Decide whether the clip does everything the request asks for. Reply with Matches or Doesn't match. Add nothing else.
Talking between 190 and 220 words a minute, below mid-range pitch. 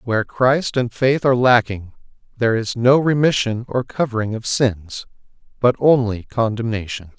Doesn't match